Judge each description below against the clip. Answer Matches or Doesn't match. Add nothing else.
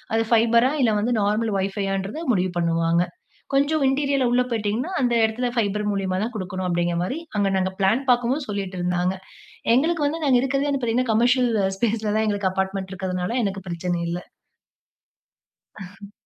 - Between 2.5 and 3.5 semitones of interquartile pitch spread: Doesn't match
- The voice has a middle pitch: Doesn't match